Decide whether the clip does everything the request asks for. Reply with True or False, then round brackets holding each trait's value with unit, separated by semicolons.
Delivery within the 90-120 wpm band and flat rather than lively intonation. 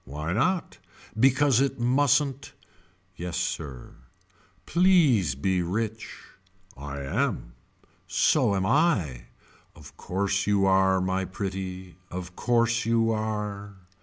False (105 wpm; 4.8 semitones)